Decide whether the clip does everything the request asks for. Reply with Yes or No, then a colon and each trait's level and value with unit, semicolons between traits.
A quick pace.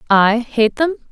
No: average, 160 wpm